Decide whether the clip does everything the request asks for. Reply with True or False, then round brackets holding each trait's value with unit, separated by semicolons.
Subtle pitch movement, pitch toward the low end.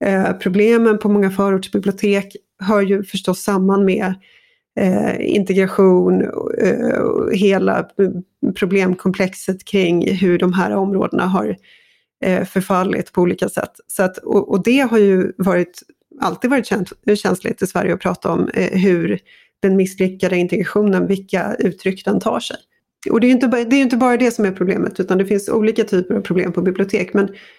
False (2.1 semitones; 195 Hz)